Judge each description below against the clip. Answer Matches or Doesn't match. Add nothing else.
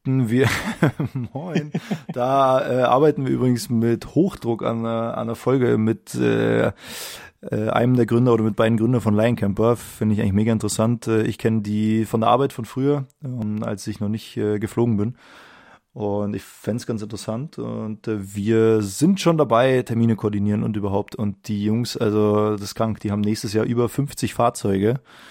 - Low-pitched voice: Matches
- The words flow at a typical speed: Matches